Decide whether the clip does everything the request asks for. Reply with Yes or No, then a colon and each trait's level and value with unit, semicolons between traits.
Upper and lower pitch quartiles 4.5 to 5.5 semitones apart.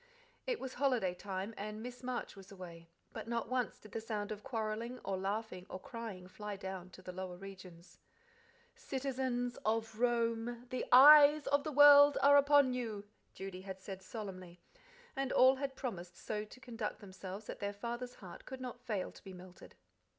Yes: average, 4.9 semitones